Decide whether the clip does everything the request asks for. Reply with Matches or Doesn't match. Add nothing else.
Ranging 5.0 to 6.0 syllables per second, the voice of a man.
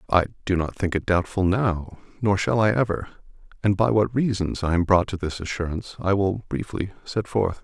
Matches